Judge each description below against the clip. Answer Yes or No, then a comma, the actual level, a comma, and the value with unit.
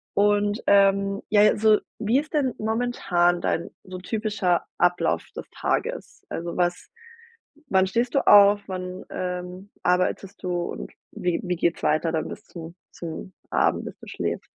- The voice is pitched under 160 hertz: No, high, 190 Hz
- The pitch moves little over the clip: No, average, 3.0 semitones